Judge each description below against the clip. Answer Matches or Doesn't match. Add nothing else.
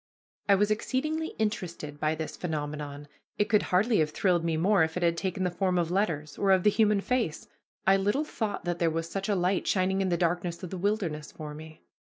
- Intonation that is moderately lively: Matches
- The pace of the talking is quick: Matches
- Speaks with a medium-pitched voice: Matches